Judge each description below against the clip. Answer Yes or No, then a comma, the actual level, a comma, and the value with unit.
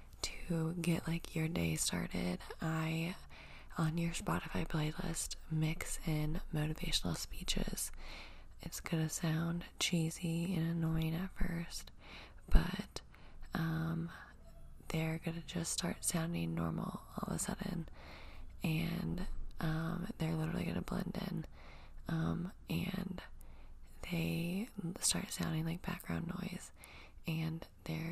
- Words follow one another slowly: Yes, slow, 110 wpm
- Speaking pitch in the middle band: Yes, medium, 160 Hz